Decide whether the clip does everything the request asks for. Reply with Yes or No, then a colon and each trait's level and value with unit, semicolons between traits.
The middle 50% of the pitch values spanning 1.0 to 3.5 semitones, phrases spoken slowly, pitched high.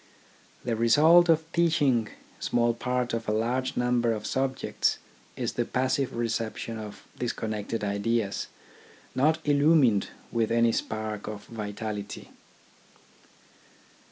No: average, 3.2 semitones; slow, 110 wpm; low, 115 Hz